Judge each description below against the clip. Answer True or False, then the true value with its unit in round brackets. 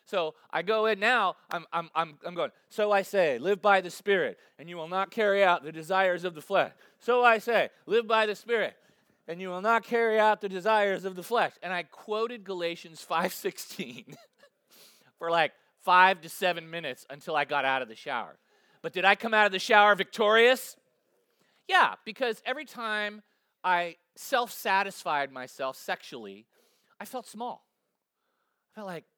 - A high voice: True (195 Hz)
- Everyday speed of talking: True (180 wpm)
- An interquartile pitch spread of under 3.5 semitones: False (4.4 semitones)